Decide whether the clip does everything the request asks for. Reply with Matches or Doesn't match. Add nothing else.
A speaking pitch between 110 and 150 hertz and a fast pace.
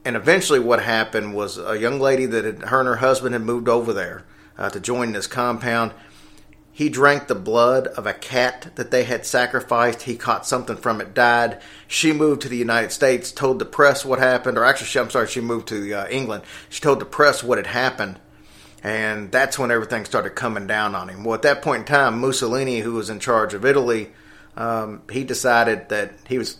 Matches